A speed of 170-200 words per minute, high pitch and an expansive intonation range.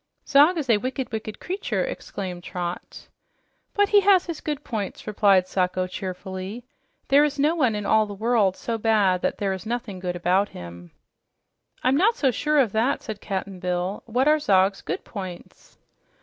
Yes: average, 180 wpm; high, 215 Hz; wide, 6.7 semitones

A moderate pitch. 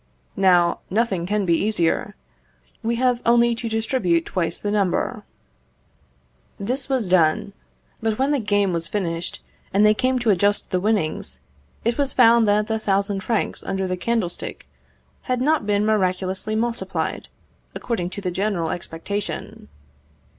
No: high, 205 Hz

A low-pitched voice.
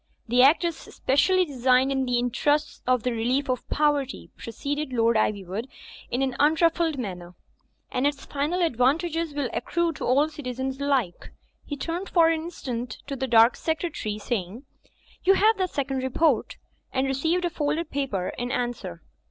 No: very high, 270 Hz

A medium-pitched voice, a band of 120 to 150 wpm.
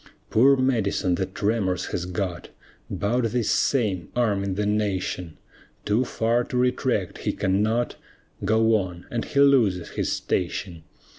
No: low, 105 Hz; slow, 135 wpm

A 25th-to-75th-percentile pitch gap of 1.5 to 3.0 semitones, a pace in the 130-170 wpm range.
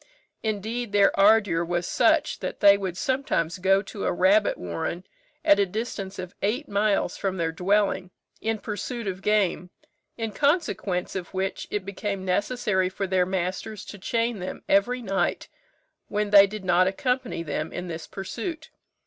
Yes: average, 2.7 semitones; average, 160 wpm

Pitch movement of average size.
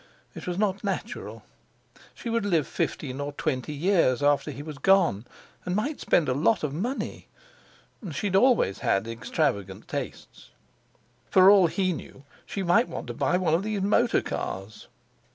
No: wide, 6.1 semitones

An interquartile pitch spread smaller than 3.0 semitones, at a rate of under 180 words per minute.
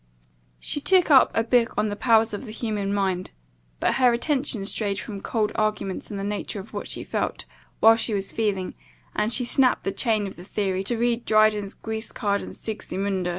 No: narrow, 2.6 semitones; average, 195 wpm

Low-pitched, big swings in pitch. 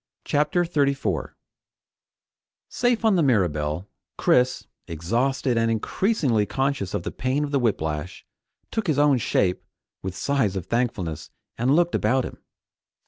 Yes: low, 125 Hz; wide, 7.3 semitones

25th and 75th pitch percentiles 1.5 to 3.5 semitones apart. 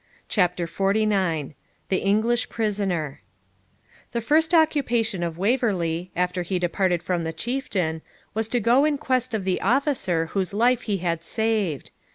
No: average, 5.2 semitones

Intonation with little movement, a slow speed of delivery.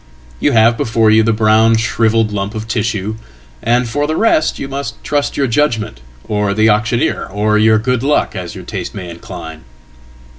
No: narrow, 2.1 semitones; average, 160 wpm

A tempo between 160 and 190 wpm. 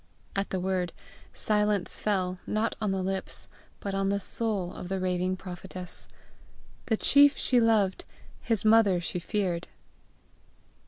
No: average, 140 wpm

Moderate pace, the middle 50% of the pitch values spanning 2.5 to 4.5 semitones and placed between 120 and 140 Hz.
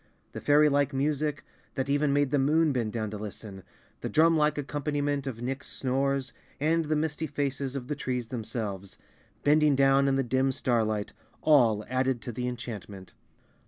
Yes: average, 165 wpm; average, 3.1 semitones; low, 135 Hz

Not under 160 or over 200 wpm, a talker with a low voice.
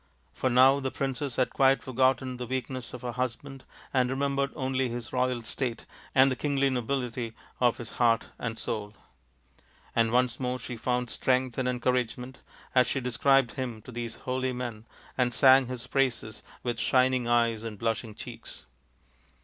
Yes: average, 165 wpm; low, 125 Hz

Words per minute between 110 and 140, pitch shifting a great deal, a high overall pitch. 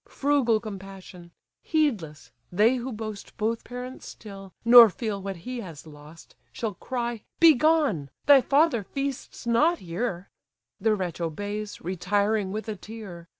No: slow, 135 wpm; average, 4.7 semitones; high, 215 Hz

